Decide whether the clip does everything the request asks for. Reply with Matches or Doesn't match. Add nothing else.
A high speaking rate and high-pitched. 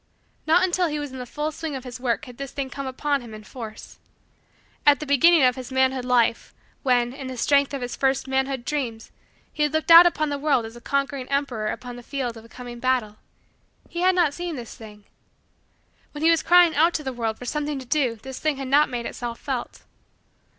Matches